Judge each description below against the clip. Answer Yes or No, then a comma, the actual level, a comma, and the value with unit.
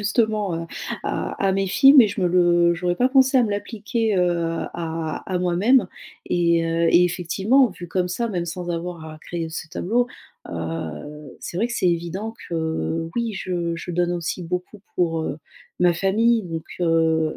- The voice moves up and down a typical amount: Yes, average, 3.6 semitones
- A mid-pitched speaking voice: Yes, medium, 175 Hz